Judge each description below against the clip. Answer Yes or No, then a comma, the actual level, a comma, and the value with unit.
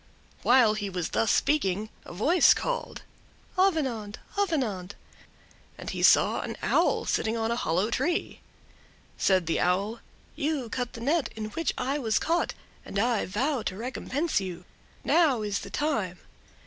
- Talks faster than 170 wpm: No, average, 150 wpm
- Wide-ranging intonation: Yes, wide, 6.4 semitones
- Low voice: No, high, 230 Hz